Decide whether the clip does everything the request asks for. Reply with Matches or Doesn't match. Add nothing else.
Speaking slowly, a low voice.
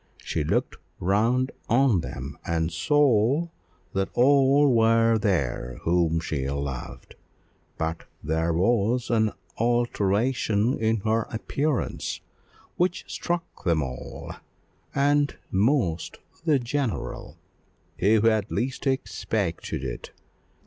Matches